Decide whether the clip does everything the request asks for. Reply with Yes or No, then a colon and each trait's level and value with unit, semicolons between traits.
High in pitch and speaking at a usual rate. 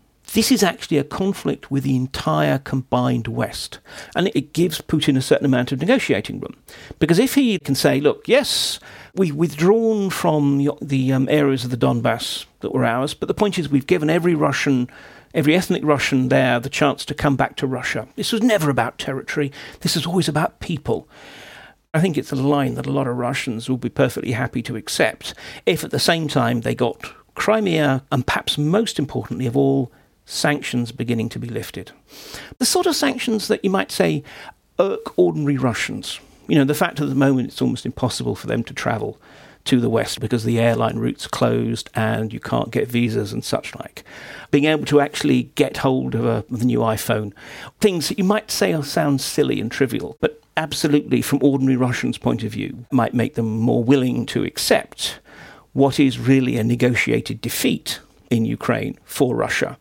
No: medium, 140 Hz; average, 190 wpm